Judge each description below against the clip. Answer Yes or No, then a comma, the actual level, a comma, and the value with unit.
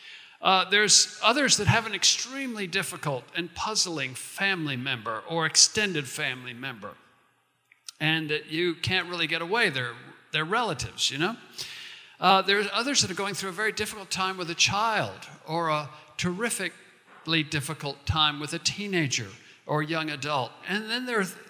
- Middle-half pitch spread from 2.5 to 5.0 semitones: No, wide, 5.5 semitones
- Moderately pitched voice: Yes, medium, 175 Hz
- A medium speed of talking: Yes, average, 160 wpm